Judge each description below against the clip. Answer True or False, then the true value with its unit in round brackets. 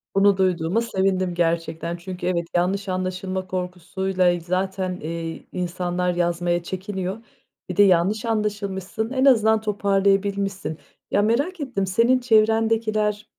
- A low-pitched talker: False (190 Hz)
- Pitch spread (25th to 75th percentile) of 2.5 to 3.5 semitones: True (2.9 semitones)